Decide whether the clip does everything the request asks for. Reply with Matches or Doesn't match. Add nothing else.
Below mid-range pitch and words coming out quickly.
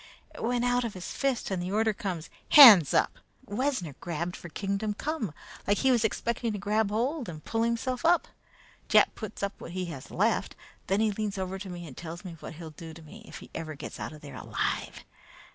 Doesn't match